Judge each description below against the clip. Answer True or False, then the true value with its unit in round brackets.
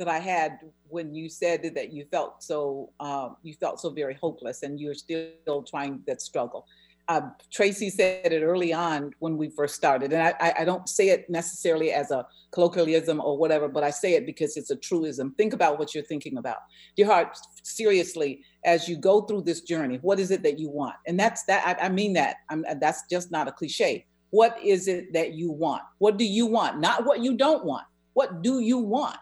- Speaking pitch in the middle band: True (165 Hz)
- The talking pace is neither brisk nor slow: False (215 wpm)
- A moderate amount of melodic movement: True (4.1 semitones)